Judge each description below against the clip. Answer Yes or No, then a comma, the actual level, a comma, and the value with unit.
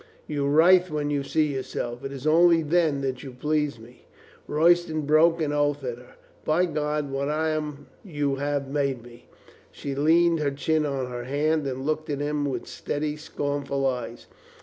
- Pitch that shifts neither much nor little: No, narrow, 2.1 semitones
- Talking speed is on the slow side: No, average, 175 wpm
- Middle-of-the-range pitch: Yes, medium, 145 Hz